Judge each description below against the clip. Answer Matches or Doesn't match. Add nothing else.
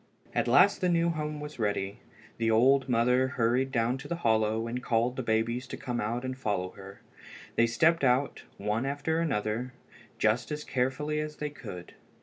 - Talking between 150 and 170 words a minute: Doesn't match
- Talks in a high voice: Doesn't match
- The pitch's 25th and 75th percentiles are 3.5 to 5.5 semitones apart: Matches